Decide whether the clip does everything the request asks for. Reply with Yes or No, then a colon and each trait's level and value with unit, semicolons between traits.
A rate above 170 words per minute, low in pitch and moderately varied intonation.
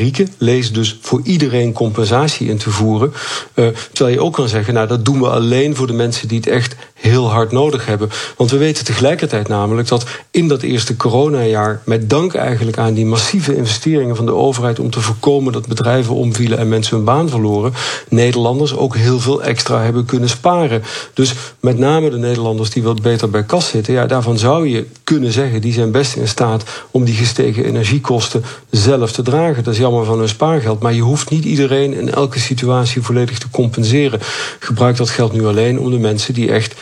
Yes: fast, 200 wpm; low, 120 Hz; average, 3.1 semitones